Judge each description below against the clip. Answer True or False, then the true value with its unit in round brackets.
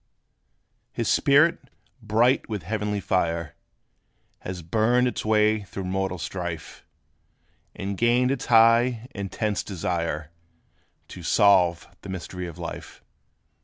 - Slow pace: True (110 wpm)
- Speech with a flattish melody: False (4.2 semitones)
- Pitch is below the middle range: True (100 Hz)